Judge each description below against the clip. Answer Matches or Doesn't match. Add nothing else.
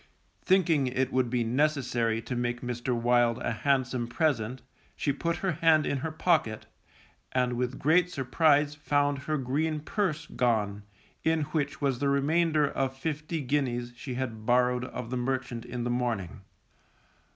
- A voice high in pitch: Doesn't match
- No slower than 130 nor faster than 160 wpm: Matches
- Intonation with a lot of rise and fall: Doesn't match